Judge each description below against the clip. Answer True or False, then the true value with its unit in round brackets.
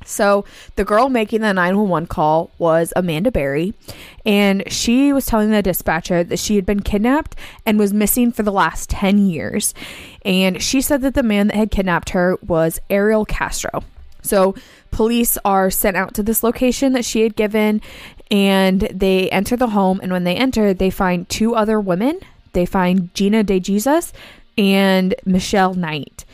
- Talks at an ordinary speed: True (175 wpm)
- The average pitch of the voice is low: False (200 Hz)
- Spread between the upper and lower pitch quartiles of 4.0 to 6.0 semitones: False (3.0 semitones)